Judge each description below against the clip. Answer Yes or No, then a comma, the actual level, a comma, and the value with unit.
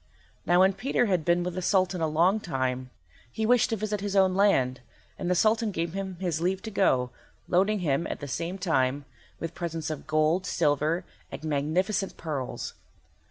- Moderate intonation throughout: Yes, average, 4.1 semitones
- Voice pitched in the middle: Yes, medium, 175 Hz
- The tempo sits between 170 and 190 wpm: Yes, average, 185 wpm